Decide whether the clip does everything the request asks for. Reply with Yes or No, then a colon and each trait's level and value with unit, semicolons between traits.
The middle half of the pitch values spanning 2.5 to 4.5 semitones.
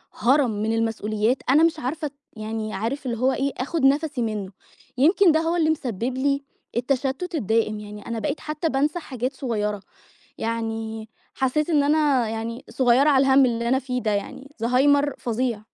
Yes: average, 4.2 semitones